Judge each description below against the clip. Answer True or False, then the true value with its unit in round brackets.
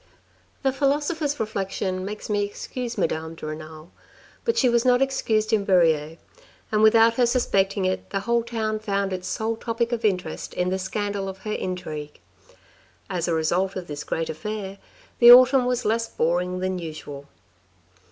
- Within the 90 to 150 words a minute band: False (165 wpm)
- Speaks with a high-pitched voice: True (200 Hz)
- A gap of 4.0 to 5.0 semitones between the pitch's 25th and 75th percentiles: True (4.4 semitones)